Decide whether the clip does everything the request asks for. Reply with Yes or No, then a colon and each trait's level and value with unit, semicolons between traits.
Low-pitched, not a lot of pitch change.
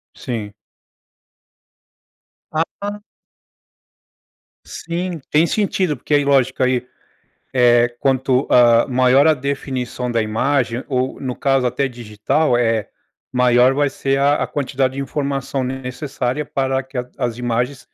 Yes: low, 130 Hz; narrow, 2.3 semitones